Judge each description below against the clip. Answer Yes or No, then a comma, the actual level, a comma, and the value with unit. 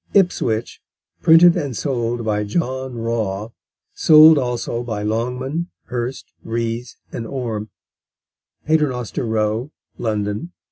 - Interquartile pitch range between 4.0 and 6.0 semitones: No, average, 3.6 semitones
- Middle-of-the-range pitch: No, low, 120 Hz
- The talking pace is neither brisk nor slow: No, slow, 100 wpm